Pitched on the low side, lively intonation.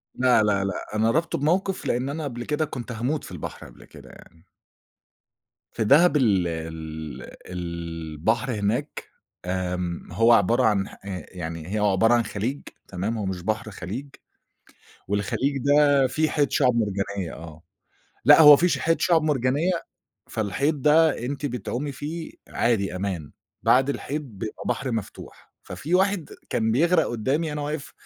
Yes: low, 115 Hz; wide, 7.0 semitones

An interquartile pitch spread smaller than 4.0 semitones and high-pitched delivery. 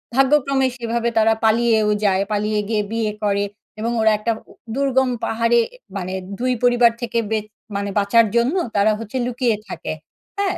Yes: average, 2.7 semitones; high, 230 Hz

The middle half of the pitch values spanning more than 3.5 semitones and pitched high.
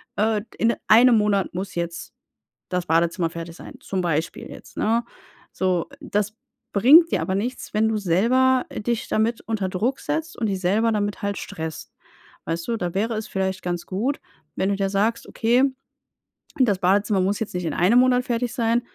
Yes: average, 4.0 semitones; high, 205 Hz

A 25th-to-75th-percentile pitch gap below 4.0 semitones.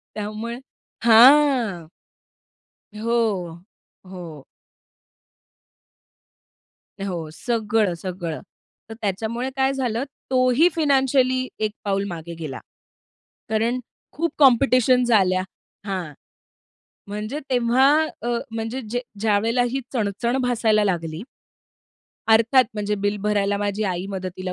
No: average, 4.3 semitones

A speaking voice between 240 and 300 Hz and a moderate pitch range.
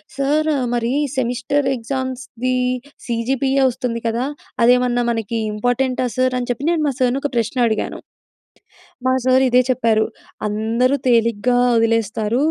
No: high, 245 Hz; narrow, 2.0 semitones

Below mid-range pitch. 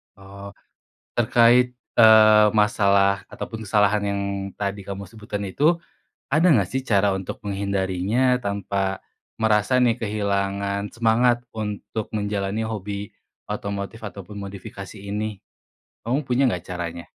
Yes: low, 105 Hz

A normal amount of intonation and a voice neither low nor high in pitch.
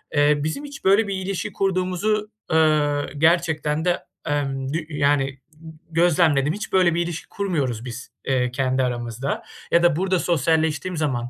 Yes: average, 4.5 semitones; medium, 155 Hz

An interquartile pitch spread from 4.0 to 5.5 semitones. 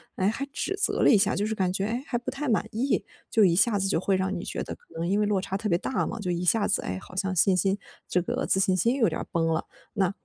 No: average, 3.5 semitones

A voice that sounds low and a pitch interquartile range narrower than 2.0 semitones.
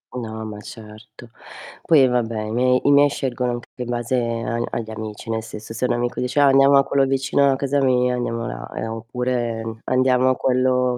No: low, 125 Hz; narrow, 2.4 semitones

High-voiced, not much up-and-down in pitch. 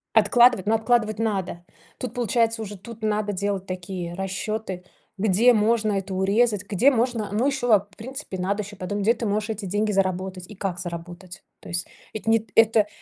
No: high, 205 Hz; average, 3.0 semitones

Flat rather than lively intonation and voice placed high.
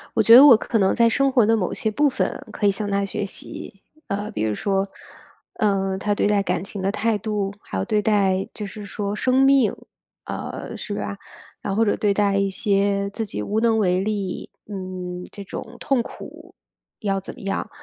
Yes: narrow, 1.9 semitones; high, 205 Hz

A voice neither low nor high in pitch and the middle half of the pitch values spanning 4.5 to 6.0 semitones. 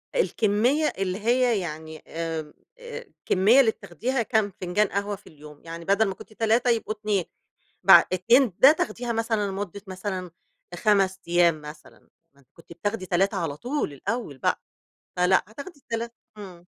No: high, 200 Hz; average, 4.8 semitones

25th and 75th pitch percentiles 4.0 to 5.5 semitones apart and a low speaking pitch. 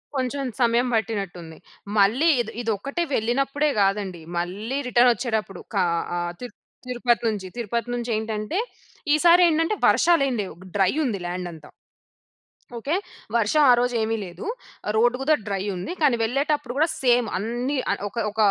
No: average, 5.1 semitones; high, 235 Hz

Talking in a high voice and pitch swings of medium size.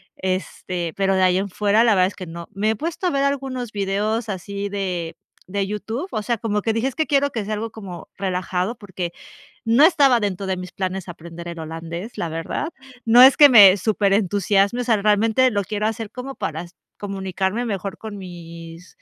Yes: high, 200 Hz; average, 3.6 semitones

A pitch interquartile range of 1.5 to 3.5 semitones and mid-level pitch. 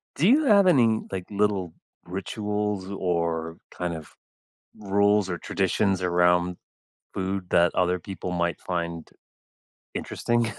No: average, 2.9 semitones; very low, 95 Hz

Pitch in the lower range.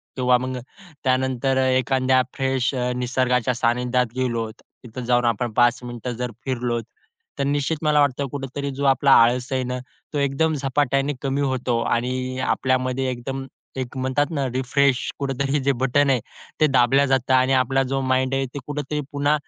Yes: low, 130 Hz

